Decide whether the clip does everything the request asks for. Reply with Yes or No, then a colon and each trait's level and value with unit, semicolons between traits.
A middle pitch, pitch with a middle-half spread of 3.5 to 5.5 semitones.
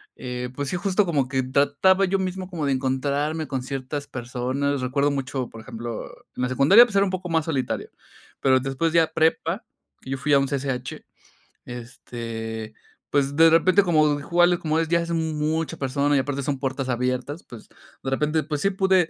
Yes: medium, 145 Hz; average, 4.0 semitones